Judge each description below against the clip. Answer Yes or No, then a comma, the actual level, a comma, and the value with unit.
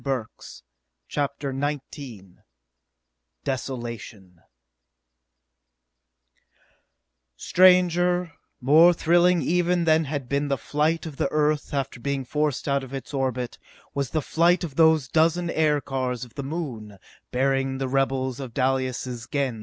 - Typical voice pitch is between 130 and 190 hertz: Yes, medium, 140 Hz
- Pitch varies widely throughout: No, average, 3.6 semitones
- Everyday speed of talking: No, slow, 130 wpm